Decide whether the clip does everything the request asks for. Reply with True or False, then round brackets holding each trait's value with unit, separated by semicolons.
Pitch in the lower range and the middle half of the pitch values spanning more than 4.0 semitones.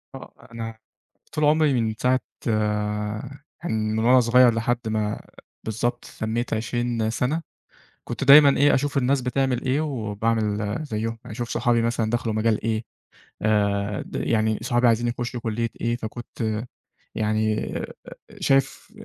False (115 Hz; 2.5 semitones)